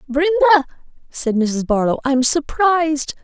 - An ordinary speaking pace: No, slow, 130 wpm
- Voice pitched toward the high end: Yes, very high, 290 Hz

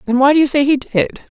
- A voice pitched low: No, very high, 270 Hz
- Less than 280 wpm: No, fast, 300 wpm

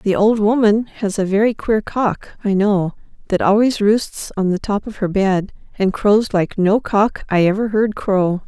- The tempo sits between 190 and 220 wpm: Yes, average, 200 wpm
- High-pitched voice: Yes, high, 205 Hz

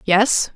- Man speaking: No, female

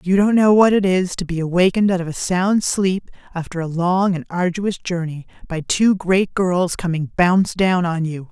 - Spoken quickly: Yes, fast, 210 wpm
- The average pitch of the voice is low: No, medium, 180 Hz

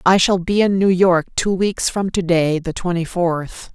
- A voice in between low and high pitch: Yes, medium, 180 Hz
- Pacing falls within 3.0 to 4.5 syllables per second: Yes, 4.2 syllables/s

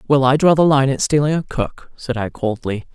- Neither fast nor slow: No, fast, 245 wpm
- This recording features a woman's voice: Yes, female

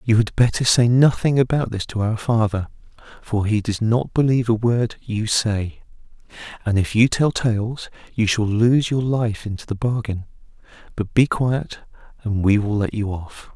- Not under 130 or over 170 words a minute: No, average, 180 wpm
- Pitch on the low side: Yes, low, 110 Hz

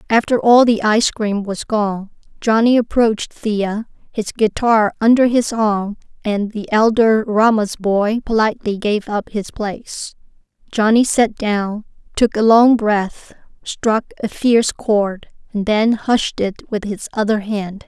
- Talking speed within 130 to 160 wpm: Yes, average, 150 wpm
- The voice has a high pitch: Yes, high, 215 Hz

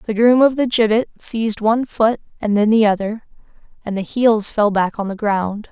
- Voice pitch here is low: No, high, 220 Hz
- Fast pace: Yes, fast, 210 wpm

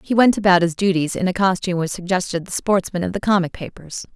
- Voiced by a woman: Yes, female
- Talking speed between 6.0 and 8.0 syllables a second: Yes, 6.3 syllables/s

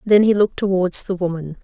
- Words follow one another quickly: Yes, fast, 220 wpm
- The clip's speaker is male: No, female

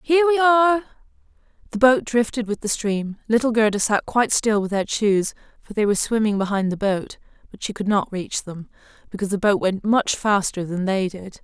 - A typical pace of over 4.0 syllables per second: Yes, 5.4 syllables/s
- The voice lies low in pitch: No, high, 220 Hz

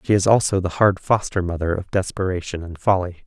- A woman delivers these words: No, male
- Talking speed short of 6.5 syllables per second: Yes, 5.7 syllables/s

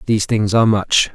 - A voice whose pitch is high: No, low, 110 Hz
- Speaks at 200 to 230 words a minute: Yes, fast, 210 wpm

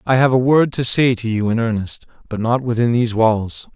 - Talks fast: Yes, fast, 240 wpm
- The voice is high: No, low, 115 Hz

